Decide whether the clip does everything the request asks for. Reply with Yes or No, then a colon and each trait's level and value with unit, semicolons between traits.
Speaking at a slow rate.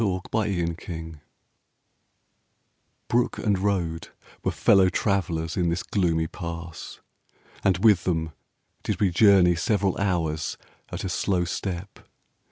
Yes: slow, 120 wpm